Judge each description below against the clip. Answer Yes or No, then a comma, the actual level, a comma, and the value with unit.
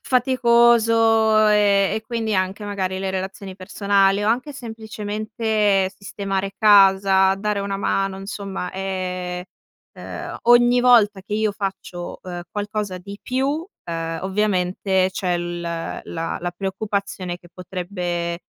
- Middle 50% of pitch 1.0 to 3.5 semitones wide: Yes, narrow, 2.4 semitones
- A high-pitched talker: Yes, high, 200 Hz